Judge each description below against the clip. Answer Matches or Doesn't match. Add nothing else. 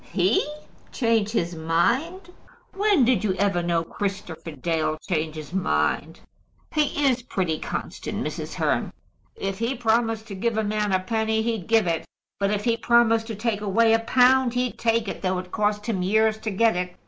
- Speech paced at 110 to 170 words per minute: Doesn't match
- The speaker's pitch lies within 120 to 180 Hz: Doesn't match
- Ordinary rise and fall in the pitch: Matches